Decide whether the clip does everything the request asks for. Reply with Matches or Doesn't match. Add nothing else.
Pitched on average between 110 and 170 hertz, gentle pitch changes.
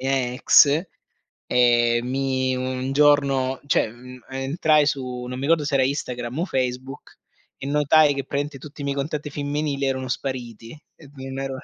Matches